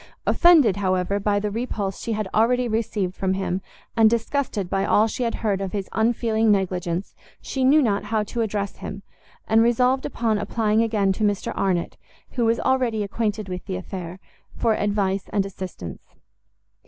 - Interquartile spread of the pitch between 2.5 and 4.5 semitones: Yes, average, 2.9 semitones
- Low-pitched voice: No, high, 210 Hz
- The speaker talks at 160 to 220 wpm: Yes, average, 170 wpm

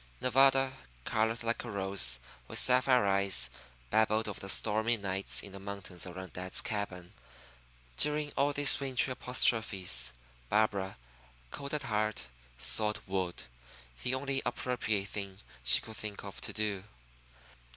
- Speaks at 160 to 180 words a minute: No, slow, 135 wpm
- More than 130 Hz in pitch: No, low, 105 Hz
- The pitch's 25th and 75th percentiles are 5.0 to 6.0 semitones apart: No, average, 4.5 semitones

